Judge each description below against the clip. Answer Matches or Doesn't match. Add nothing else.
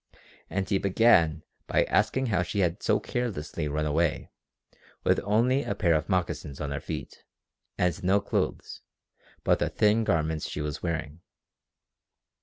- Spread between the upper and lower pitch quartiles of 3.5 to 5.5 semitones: Matches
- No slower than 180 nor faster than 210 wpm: Doesn't match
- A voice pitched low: Matches